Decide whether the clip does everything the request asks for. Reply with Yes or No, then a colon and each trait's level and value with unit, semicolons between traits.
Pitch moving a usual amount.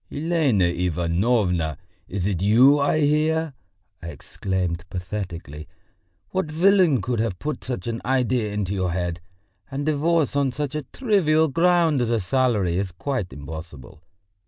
No: wide, 8.8 semitones